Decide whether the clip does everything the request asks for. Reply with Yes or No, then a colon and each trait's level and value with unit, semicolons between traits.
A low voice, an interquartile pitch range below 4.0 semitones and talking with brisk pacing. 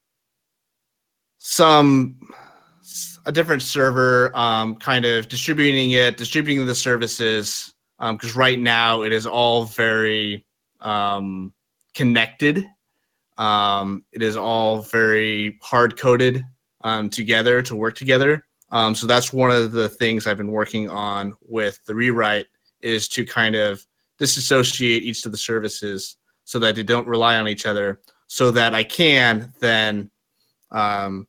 No: low, 115 Hz; average, 2.7 semitones; slow, 135 wpm